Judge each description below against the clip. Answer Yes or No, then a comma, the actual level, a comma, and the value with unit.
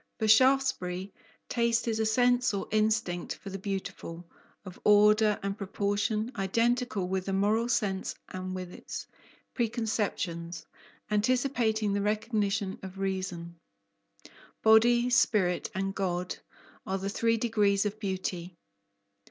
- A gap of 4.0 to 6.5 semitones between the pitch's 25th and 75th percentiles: No, average, 2.9 semitones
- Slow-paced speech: Yes, slow, 120 wpm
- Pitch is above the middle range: Yes, high, 205 Hz